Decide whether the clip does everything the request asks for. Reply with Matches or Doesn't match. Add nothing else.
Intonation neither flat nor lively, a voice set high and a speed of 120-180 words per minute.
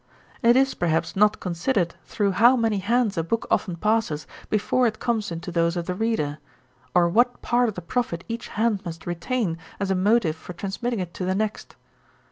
Doesn't match